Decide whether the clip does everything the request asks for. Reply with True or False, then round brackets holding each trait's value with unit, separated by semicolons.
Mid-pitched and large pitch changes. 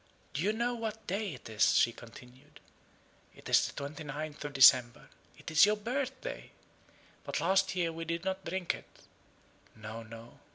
True (160 Hz; 7.6 semitones)